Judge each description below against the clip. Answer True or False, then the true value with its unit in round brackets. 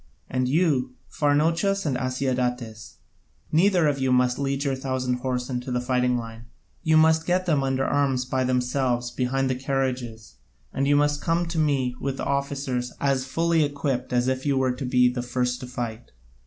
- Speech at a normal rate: True (180 wpm)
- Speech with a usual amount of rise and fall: False (2.3 semitones)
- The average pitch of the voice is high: False (130 Hz)